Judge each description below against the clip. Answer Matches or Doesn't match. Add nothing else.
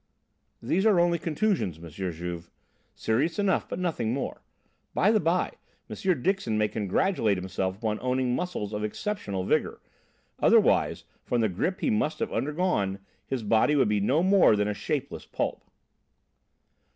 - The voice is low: Matches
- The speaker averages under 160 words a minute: Matches